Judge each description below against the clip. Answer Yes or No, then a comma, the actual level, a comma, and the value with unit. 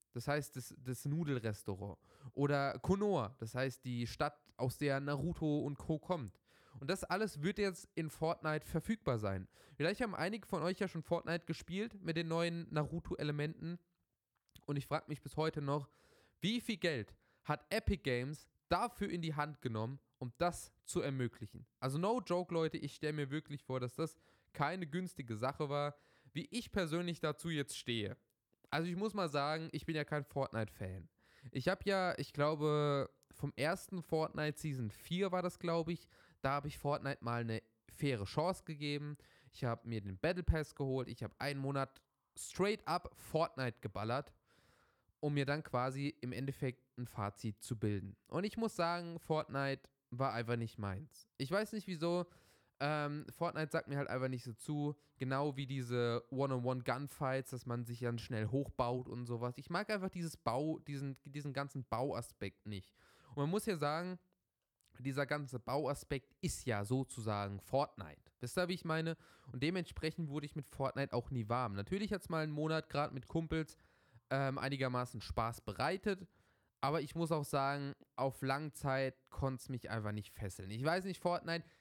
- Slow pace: No, average, 175 wpm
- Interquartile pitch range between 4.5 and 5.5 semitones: Yes, average, 4.8 semitones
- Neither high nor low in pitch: Yes, medium, 145 Hz